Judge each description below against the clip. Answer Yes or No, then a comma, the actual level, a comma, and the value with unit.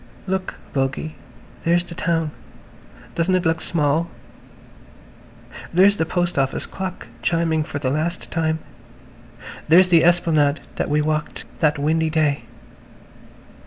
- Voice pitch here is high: No, medium, 160 Hz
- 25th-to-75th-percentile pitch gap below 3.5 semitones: Yes, narrow, 2.4 semitones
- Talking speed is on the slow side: Yes, slow, 125 wpm